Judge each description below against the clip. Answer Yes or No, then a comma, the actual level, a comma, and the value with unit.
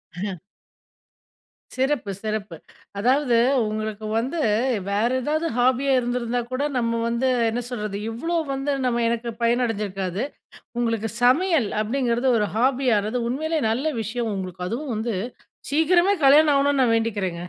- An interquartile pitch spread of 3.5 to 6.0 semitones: Yes, average, 3.9 semitones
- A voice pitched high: Yes, high, 240 Hz